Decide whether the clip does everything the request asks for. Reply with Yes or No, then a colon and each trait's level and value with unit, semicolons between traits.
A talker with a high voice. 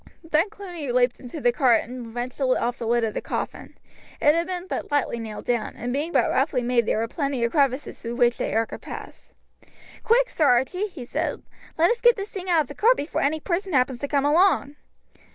Yes: very high, 280 Hz